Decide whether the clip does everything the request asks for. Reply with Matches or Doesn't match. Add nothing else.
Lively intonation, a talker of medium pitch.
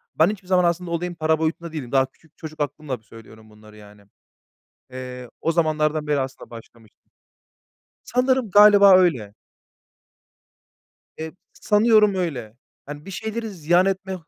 Matches